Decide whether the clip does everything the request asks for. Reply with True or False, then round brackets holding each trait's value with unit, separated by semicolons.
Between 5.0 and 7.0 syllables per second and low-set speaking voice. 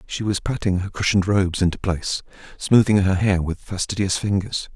True (5.4 syllables/s; 95 Hz)